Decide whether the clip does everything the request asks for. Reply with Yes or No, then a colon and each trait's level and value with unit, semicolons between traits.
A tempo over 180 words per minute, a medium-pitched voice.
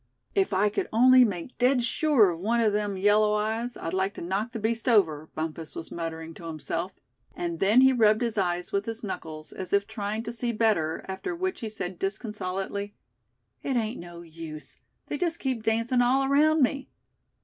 No: average, 195 wpm; high, 210 Hz